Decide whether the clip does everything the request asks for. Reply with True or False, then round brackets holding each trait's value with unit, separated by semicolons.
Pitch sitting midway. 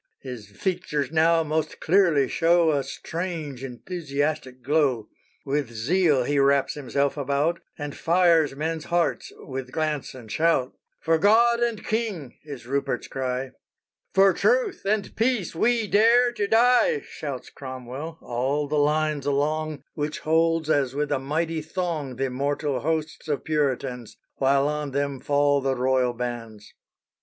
True (150 Hz)